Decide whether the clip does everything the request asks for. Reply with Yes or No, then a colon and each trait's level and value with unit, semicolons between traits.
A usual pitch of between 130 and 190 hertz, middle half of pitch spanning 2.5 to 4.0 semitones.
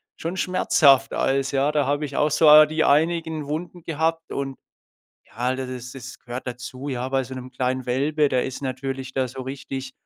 Yes: low, 135 Hz; average, 2.9 semitones